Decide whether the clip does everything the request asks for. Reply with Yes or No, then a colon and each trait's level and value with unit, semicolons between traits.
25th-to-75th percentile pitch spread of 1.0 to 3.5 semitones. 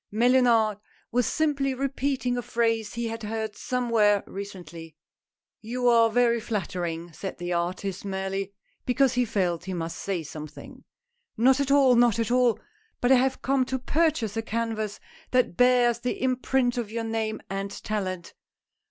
No: average, 4.1 semitones